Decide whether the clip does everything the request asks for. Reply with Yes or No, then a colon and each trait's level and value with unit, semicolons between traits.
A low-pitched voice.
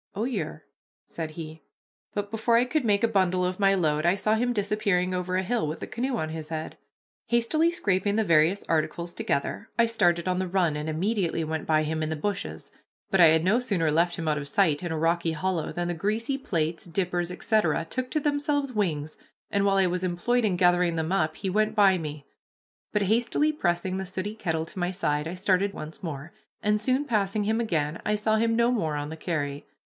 No: medium, 185 Hz